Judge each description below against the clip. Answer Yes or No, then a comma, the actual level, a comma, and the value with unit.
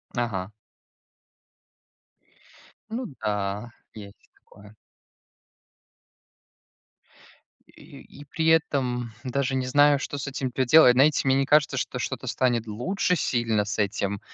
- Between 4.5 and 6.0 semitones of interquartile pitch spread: Yes, average, 5.0 semitones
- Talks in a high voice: No, low, 125 Hz